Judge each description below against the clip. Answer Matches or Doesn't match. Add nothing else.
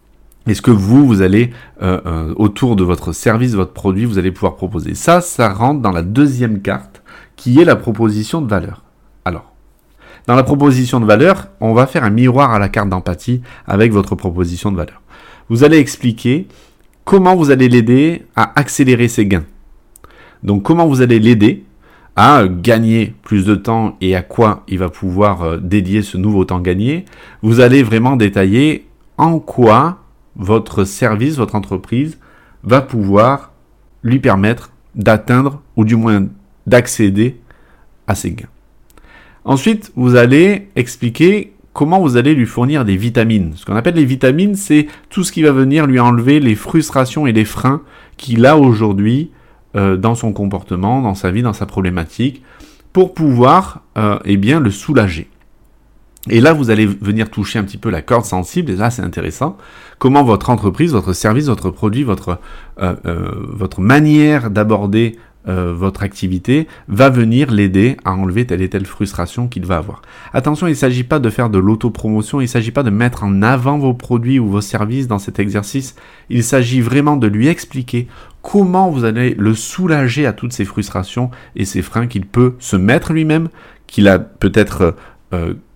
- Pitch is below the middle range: Matches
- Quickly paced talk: Doesn't match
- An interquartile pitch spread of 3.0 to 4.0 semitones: Doesn't match